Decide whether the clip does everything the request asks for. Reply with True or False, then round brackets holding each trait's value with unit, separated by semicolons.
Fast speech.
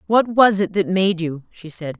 True (240 wpm)